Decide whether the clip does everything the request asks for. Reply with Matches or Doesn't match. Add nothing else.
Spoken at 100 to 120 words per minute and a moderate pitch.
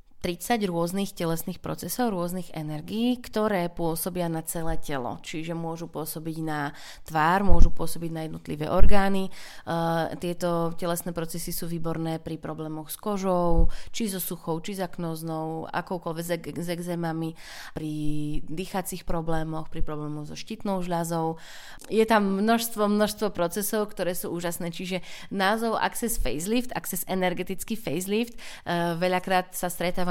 Doesn't match